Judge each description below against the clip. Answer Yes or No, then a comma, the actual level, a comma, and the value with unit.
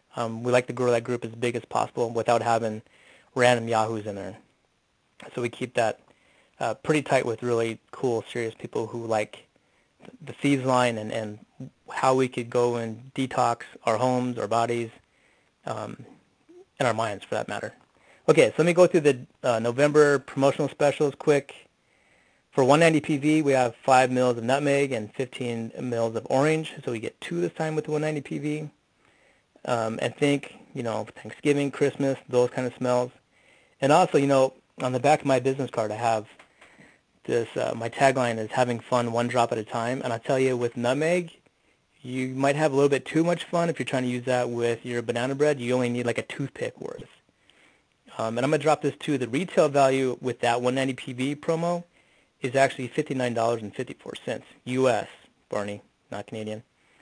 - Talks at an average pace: Yes, average, 190 wpm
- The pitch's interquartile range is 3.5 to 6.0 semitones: No, average, 3.1 semitones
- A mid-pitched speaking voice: No, low, 125 Hz